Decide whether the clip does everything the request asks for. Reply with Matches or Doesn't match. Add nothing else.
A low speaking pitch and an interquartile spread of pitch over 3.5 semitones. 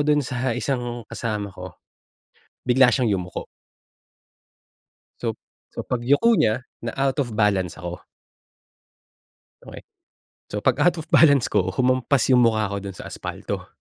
Matches